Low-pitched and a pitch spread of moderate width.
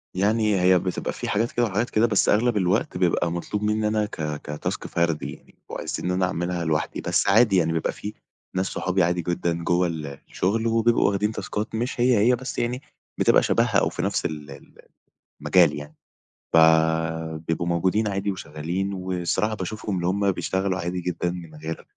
Yes: very low, 90 Hz; average, 4.0 semitones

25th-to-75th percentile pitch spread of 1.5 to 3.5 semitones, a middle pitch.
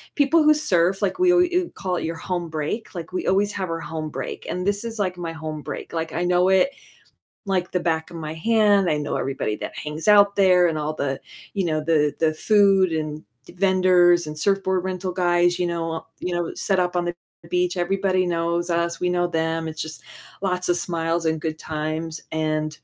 Yes: average, 2.8 semitones; medium, 175 Hz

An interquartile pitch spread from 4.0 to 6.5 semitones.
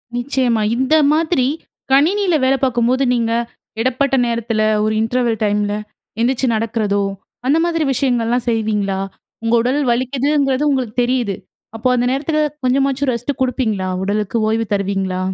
No: average, 3.4 semitones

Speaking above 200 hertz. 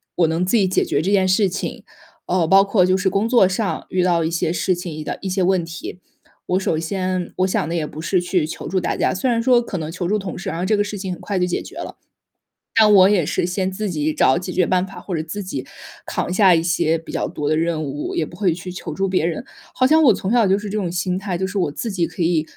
No: medium, 185 Hz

